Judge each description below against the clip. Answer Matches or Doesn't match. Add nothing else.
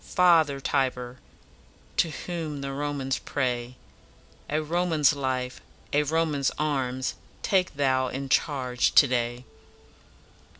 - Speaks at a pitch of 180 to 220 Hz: Doesn't match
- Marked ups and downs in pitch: Doesn't match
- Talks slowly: Matches